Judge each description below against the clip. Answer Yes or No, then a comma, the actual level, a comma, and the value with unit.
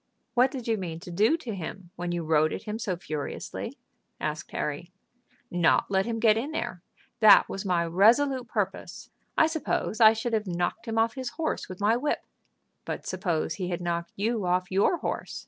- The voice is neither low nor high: No, high, 200 Hz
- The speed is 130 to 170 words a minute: No, average, 195 wpm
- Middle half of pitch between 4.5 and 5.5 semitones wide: Yes, average, 4.8 semitones